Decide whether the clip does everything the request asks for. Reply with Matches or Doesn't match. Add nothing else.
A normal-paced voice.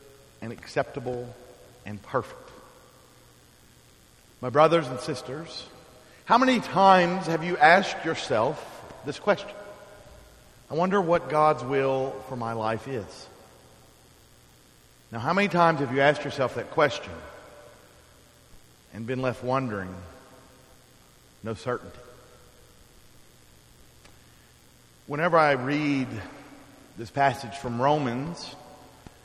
Doesn't match